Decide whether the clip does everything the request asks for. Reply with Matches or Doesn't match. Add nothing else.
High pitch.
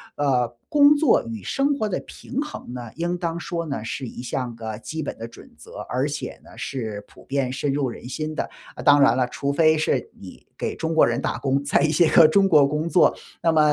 Doesn't match